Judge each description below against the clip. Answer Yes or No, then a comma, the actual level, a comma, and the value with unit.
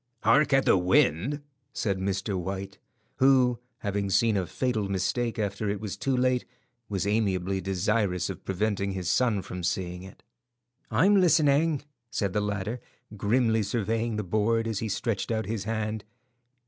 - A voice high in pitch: No, low, 105 Hz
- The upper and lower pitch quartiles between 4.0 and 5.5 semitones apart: No, average, 3.4 semitones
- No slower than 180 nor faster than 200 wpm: No, average, 155 wpm